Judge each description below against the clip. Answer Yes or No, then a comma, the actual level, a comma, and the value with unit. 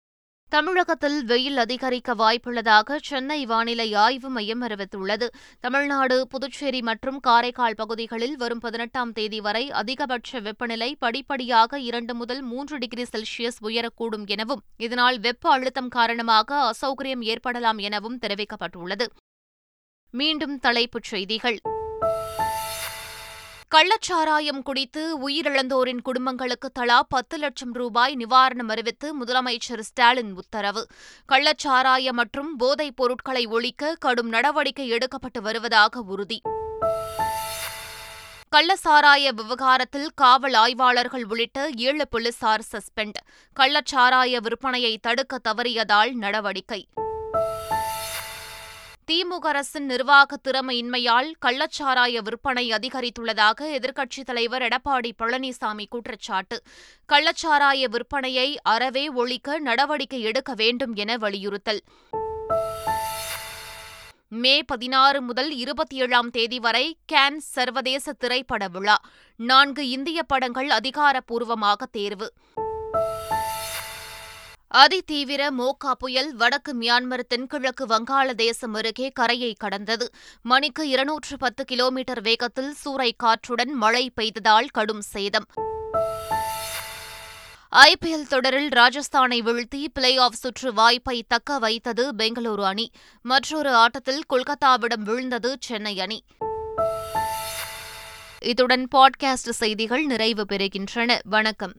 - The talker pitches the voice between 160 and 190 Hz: No, high, 245 Hz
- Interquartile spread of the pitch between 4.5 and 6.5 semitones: No, average, 3.3 semitones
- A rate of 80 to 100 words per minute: Yes, average, 95 wpm